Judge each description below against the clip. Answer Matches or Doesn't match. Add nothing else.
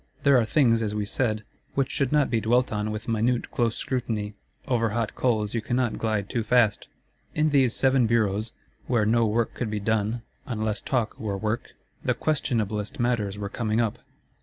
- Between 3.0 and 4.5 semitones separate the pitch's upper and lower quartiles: Doesn't match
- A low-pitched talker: Matches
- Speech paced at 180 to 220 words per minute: Matches